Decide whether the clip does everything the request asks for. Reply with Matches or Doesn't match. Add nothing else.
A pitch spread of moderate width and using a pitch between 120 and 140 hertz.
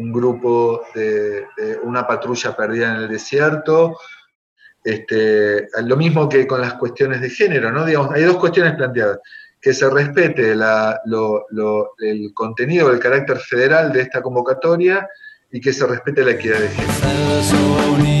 Doesn't match